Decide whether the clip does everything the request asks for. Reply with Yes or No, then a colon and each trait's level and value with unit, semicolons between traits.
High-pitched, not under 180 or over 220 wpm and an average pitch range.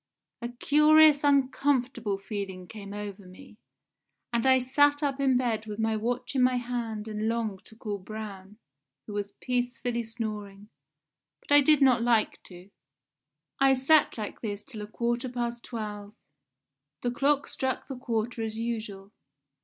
No: high, 235 Hz; average, 155 wpm; average, 3.5 semitones